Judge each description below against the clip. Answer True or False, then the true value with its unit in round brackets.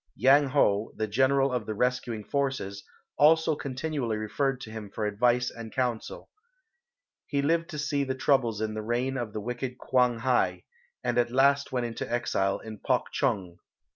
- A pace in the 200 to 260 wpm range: False (170 wpm)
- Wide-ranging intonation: False (3.8 semitones)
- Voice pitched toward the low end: True (125 Hz)